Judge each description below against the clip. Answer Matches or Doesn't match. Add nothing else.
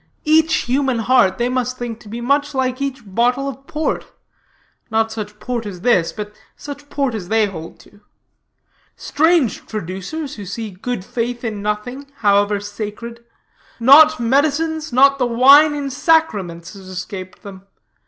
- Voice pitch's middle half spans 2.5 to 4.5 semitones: Doesn't match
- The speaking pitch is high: Matches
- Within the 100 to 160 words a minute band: Matches